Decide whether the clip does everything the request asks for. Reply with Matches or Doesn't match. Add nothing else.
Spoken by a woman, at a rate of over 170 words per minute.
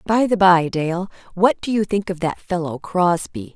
Matches